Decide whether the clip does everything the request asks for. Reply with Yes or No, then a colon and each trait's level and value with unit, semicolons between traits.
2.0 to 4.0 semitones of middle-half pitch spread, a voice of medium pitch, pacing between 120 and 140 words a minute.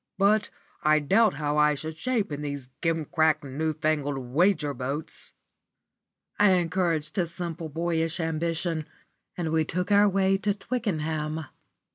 Yes: average, 3.2 semitones; medium, 160 Hz; slow, 135 wpm